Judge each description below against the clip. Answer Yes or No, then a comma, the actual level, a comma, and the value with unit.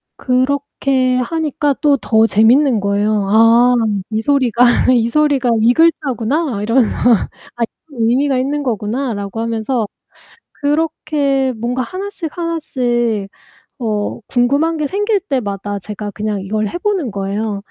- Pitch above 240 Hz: Yes, very high, 250 Hz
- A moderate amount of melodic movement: Yes, average, 4.8 semitones